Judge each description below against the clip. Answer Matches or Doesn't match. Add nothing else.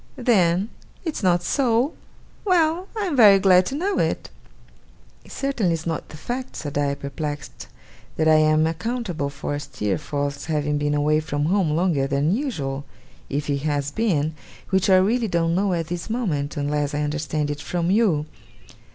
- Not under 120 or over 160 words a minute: Doesn't match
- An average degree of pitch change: Doesn't match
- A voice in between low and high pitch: Matches